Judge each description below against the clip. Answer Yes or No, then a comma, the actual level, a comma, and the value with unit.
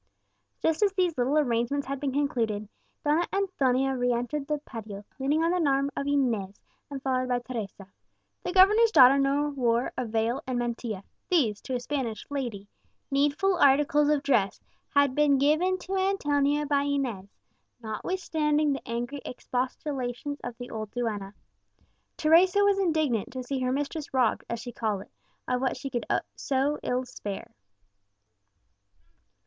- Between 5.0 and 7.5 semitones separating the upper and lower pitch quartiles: No, average, 3.6 semitones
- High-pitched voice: Yes, very high, 275 Hz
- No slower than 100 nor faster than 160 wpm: Yes, average, 155 wpm